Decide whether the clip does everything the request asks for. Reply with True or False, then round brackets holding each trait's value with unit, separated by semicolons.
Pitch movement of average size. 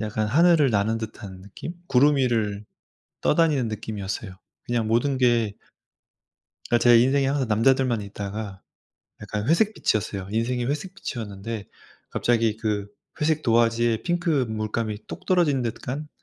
True (4.2 semitones)